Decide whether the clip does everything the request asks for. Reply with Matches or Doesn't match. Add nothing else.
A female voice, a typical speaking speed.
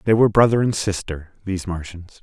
Doesn't match